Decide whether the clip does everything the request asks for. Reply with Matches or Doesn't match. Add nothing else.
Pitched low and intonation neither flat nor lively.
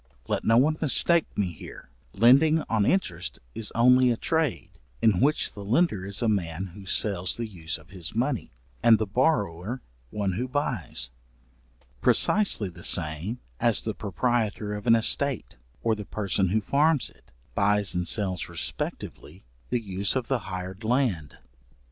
Matches